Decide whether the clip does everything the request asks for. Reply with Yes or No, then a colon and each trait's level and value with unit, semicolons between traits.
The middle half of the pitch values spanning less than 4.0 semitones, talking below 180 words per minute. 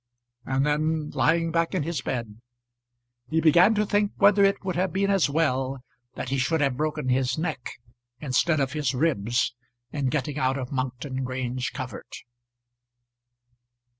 No: average, 4.3 semitones; average, 155 wpm